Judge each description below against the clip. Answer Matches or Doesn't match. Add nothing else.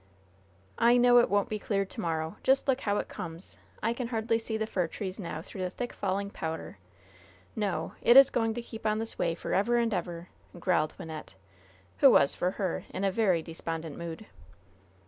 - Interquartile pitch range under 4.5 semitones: Doesn't match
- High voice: Matches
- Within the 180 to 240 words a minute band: Matches